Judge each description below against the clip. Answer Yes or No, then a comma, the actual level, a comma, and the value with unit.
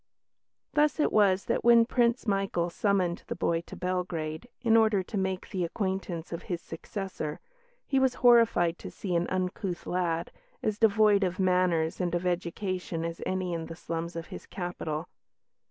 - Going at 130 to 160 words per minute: No, average, 170 wpm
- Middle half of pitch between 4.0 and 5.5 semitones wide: No, average, 3.3 semitones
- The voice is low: No, medium, 185 Hz